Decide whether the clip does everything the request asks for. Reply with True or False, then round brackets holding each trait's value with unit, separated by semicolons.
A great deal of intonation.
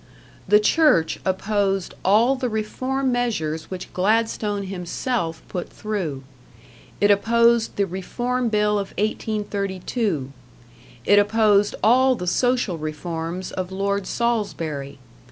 False (3.9 semitones)